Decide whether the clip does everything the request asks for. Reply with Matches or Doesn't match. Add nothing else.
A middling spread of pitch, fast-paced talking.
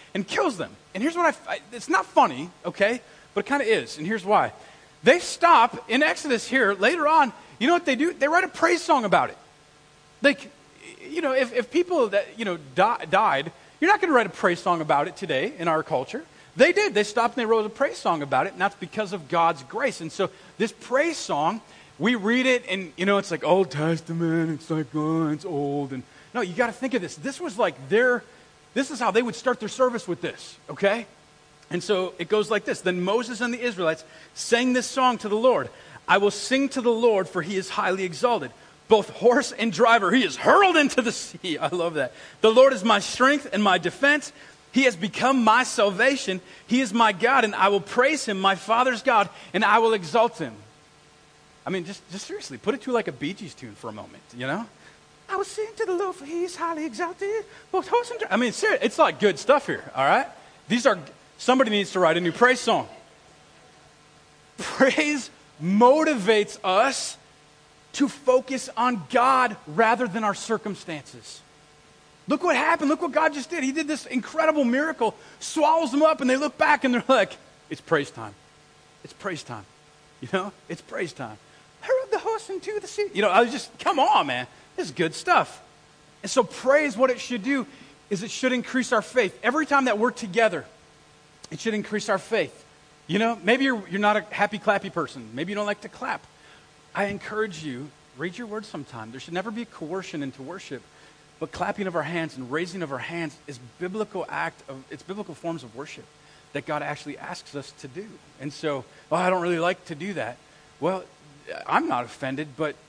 Doesn't match